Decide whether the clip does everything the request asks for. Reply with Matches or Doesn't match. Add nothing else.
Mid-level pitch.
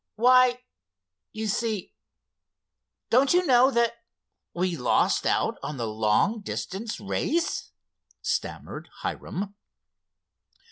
Doesn't match